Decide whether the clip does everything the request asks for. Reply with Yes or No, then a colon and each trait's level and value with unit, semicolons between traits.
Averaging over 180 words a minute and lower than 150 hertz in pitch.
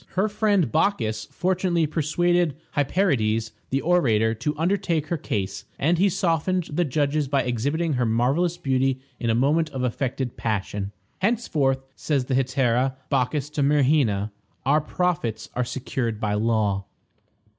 No: average, 140 wpm; medium, 140 Hz